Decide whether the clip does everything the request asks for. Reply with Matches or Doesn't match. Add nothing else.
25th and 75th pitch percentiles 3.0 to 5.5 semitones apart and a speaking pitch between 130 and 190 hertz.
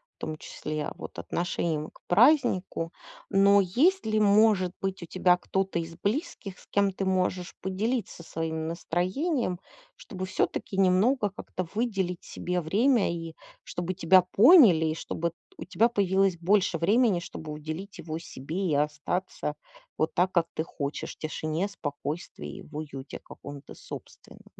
Matches